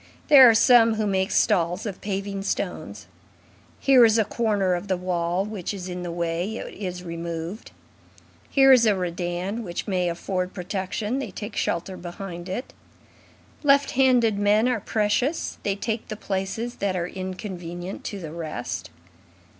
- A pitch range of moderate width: Yes, average, 3.7 semitones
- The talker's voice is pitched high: Yes, high, 195 Hz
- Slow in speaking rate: No, average, 160 wpm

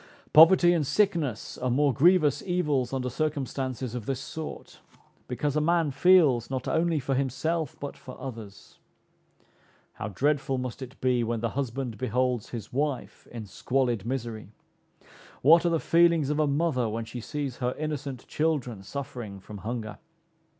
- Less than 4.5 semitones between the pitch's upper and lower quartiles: Yes, average, 4.0 semitones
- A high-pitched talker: No, low, 135 Hz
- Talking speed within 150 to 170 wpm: Yes, average, 155 wpm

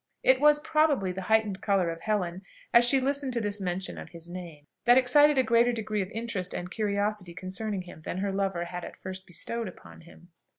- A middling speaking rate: No, fast, 210 wpm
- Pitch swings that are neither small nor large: Yes, average, 4.5 semitones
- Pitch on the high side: Yes, high, 200 Hz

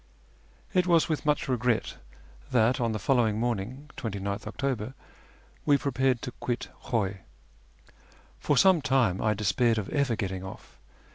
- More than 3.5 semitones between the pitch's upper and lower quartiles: Yes, average, 4.3 semitones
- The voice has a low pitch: Yes, low, 120 Hz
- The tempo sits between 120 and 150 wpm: Yes, average, 140 wpm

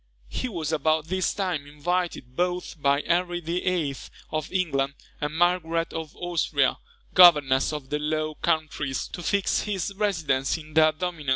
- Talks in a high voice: No, medium, 160 Hz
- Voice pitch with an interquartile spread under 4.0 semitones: Yes, average, 3.2 semitones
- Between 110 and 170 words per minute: Yes, average, 150 wpm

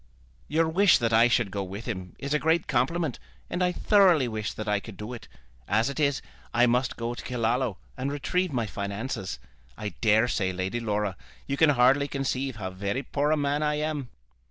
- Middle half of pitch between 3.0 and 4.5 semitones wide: No, average, 5.3 semitones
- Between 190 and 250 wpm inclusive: Yes, average, 200 wpm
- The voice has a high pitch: No, low, 125 Hz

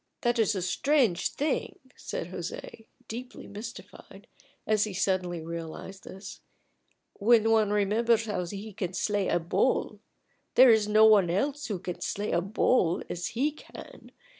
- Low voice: No, high, 210 Hz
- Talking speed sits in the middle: Yes, average, 150 wpm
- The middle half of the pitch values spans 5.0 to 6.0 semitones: No, average, 3.7 semitones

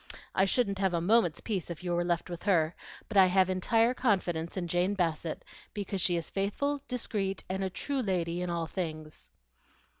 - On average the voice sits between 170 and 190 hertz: Yes, medium, 185 Hz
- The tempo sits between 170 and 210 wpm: Yes, average, 190 wpm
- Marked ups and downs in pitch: No, average, 2.7 semitones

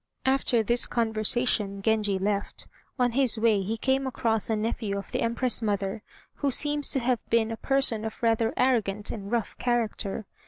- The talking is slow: No, average, 170 wpm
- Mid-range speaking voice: No, high, 225 Hz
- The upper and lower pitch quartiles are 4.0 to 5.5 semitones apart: No, narrow, 2.6 semitones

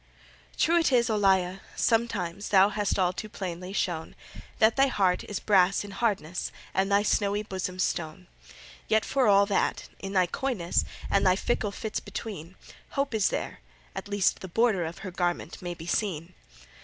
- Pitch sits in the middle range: No, high, 195 Hz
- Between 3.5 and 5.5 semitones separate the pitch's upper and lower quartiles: No, average, 2.9 semitones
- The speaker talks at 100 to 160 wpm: No, average, 170 wpm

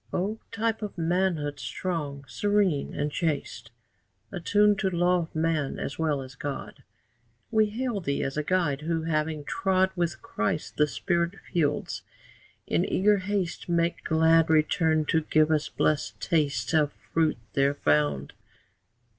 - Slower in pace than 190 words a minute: Yes, average, 145 wpm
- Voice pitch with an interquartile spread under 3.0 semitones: No, average, 3.9 semitones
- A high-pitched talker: No, medium, 160 Hz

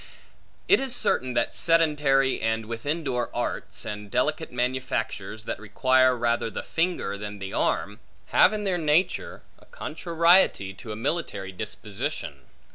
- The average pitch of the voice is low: Yes, low, 125 Hz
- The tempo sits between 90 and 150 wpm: Yes, average, 140 wpm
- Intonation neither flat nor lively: No, wide, 7.1 semitones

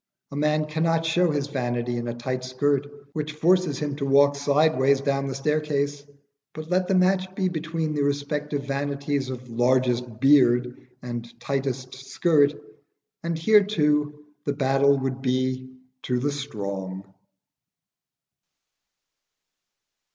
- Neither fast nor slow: No, slow, 130 wpm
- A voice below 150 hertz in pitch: Yes, medium, 140 Hz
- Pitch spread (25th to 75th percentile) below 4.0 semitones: Yes, average, 2.9 semitones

